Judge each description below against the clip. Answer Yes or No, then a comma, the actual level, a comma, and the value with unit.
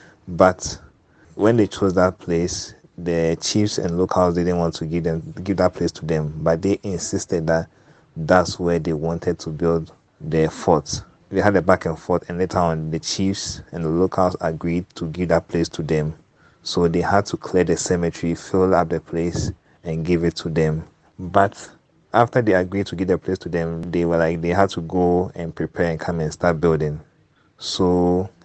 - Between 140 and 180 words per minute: No, average, 200 wpm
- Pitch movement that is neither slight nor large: No, narrow, 1.9 semitones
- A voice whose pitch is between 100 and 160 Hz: No, very low, 85 Hz